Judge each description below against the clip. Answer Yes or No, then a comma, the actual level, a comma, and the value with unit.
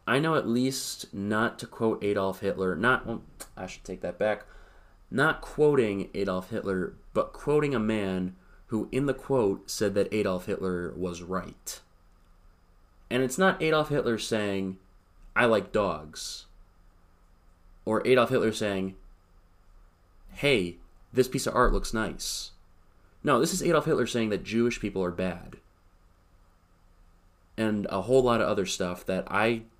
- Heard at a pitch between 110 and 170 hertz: No, very low, 95 Hz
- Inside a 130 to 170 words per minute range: Yes, average, 150 wpm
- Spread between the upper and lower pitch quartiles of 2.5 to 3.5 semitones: No, average, 4.6 semitones